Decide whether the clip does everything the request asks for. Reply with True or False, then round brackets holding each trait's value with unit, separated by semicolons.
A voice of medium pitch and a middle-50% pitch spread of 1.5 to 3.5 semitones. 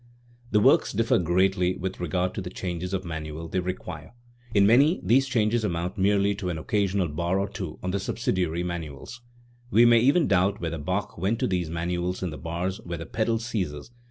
False (95 Hz; 3.1 semitones)